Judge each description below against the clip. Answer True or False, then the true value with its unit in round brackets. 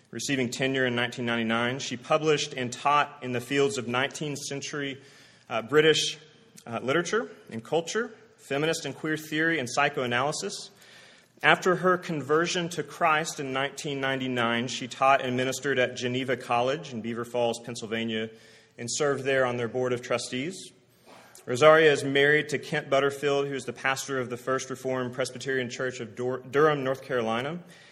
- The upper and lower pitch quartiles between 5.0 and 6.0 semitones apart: False (3.3 semitones)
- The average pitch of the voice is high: False (135 Hz)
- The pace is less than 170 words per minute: True (155 wpm)